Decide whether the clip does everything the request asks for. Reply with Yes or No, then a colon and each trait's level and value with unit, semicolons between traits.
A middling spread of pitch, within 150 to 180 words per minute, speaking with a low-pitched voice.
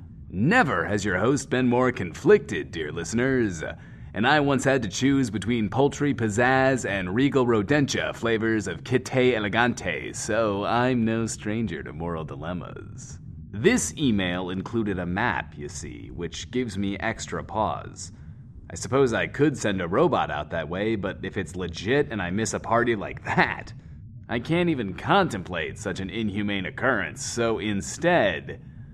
Yes: average, 4.9 semitones; average, 155 wpm; low, 110 Hz